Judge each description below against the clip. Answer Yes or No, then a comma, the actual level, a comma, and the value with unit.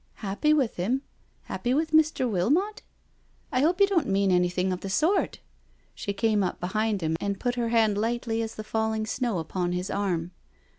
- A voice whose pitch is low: No, high, 220 Hz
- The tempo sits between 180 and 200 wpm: Yes, average, 190 wpm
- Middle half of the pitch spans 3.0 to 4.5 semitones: No, average, 5.0 semitones